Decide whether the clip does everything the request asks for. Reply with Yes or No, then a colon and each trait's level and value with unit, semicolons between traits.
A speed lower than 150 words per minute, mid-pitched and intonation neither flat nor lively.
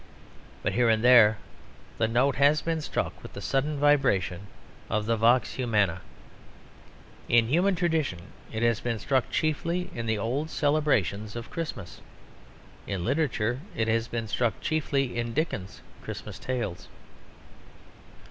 No: average, 140 wpm; low, 120 Hz; average, 4.8 semitones